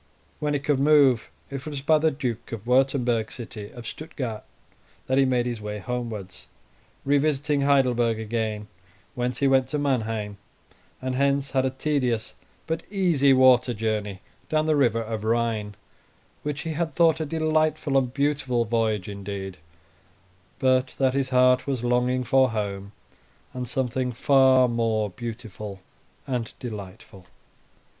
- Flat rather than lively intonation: No, average, 3.7 semitones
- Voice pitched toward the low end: Yes, low, 125 Hz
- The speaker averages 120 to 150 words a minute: Yes, average, 145 wpm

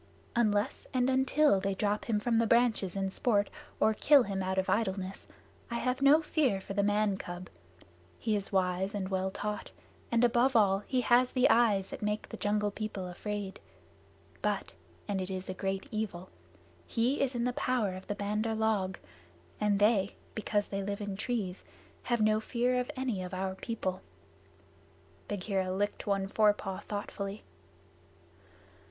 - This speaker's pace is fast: No, average, 165 wpm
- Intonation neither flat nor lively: Yes, average, 3.3 semitones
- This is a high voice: Yes, high, 205 Hz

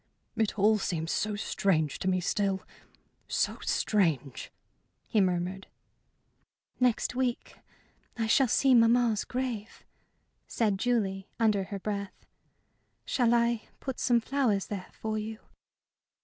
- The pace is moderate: No, slow, 120 wpm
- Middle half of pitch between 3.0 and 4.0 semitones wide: Yes, average, 3.5 semitones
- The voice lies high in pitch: Yes, high, 215 Hz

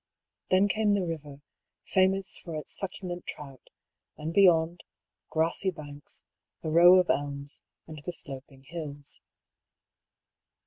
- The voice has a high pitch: No, medium, 165 Hz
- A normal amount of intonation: Yes, average, 4.2 semitones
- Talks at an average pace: No, slow, 120 wpm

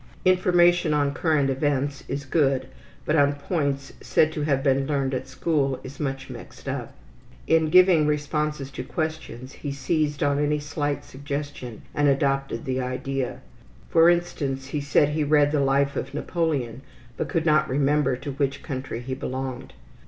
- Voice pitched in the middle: Yes, medium, 145 Hz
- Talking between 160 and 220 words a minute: Yes, average, 165 wpm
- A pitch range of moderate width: No, narrow, 2.1 semitones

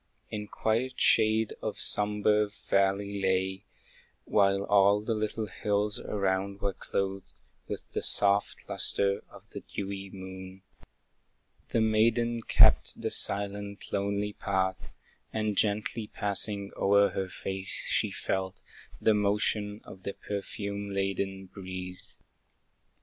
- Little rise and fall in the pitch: Yes, narrow, 1.3 semitones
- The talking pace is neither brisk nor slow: No, slow, 115 wpm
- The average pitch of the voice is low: Yes, low, 100 Hz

